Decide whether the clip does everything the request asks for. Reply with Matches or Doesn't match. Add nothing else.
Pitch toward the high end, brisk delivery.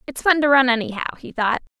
Matches